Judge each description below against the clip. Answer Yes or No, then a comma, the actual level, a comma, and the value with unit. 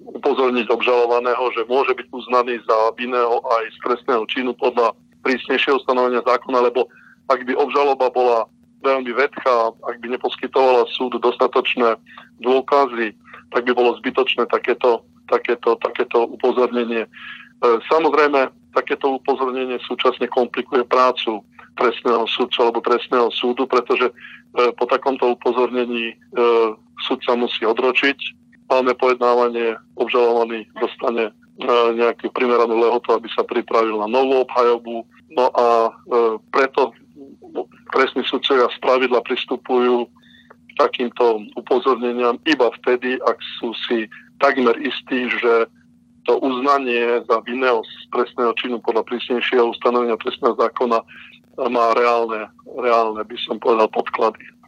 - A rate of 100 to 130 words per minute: Yes, average, 115 wpm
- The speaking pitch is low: Yes, low, 120 Hz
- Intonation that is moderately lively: No, narrow, 1.5 semitones